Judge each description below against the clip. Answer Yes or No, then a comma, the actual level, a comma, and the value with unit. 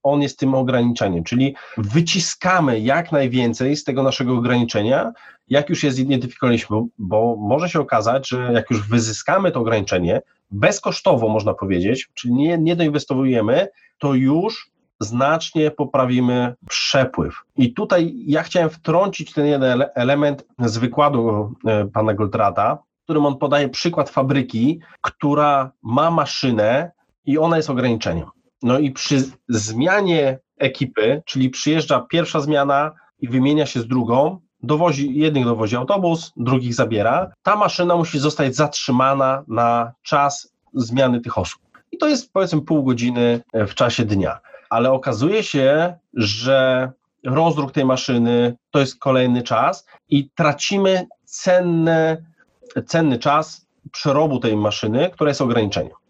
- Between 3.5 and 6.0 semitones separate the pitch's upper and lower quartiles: Yes, average, 4.2 semitones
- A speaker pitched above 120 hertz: Yes, low, 135 Hz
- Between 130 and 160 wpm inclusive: Yes, average, 135 wpm